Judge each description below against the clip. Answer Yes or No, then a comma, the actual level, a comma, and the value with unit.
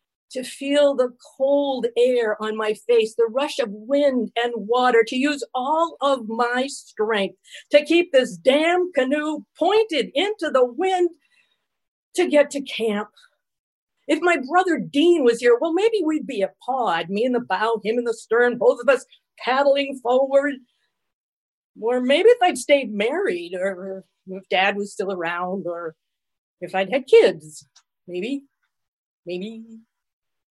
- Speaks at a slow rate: No, average, 150 wpm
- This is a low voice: No, very high, 255 Hz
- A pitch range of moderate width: No, wide, 5.9 semitones